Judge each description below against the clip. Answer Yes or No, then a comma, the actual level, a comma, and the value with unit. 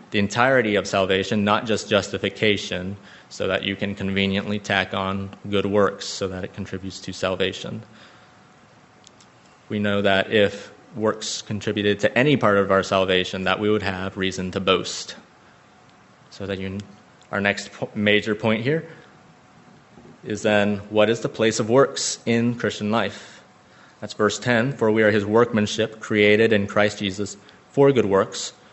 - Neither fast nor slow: Yes, average, 155 wpm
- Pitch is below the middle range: Yes, low, 105 Hz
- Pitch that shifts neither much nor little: No, narrow, 1.7 semitones